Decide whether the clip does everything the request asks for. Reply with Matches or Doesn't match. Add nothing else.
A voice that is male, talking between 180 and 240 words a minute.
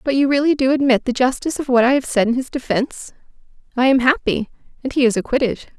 Doesn't match